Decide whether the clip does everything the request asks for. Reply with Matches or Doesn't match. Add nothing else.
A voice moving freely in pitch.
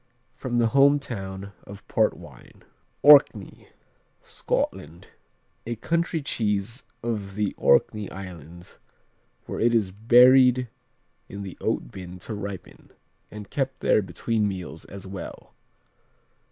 Doesn't match